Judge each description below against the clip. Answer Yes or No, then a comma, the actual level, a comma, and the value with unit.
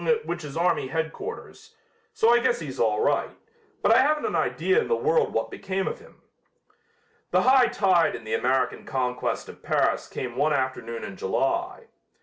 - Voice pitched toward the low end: No, high, 195 Hz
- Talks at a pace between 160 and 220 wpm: Yes, average, 175 wpm